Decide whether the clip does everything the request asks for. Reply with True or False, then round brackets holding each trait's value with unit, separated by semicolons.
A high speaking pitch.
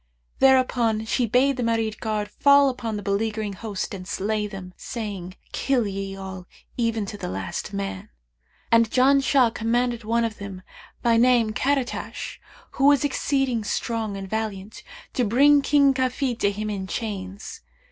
True (225 Hz)